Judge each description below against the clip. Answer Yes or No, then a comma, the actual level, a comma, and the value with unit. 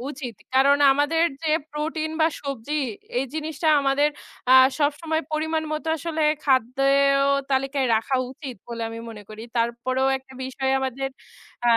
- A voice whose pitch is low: No, very high, 275 Hz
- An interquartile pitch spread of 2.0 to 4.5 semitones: Yes, average, 3.0 semitones